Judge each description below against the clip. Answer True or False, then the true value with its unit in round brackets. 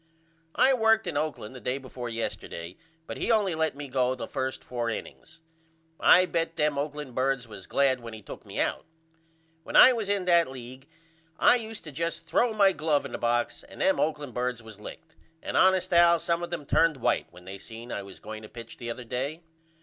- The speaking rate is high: True (215 wpm)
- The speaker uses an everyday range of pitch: False (5.9 semitones)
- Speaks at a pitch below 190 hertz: True (140 Hz)